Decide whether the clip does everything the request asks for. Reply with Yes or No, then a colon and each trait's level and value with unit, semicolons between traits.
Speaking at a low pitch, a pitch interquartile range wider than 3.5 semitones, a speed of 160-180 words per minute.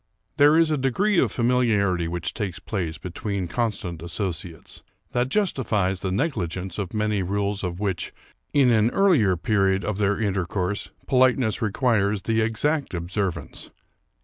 No: low, 105 Hz; average, 4.7 semitones; average, 145 wpm